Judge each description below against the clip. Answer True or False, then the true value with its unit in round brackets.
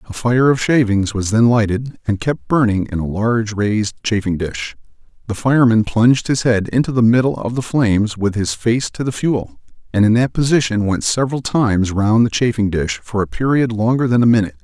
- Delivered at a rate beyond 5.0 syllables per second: True (5.5 syllables/s)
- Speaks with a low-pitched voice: True (110 Hz)